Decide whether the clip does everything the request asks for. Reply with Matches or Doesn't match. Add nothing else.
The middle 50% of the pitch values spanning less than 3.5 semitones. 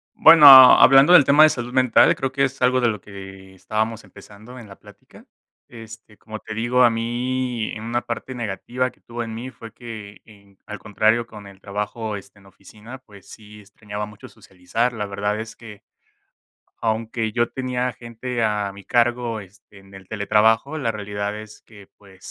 Matches